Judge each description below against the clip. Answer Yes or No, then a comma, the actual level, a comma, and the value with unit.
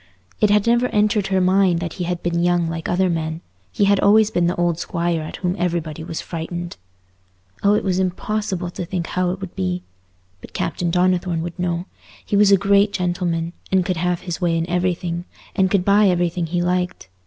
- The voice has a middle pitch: Yes, medium, 180 Hz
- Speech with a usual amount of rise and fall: No, narrow, 1.9 semitones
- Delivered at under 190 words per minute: No, fast, 205 wpm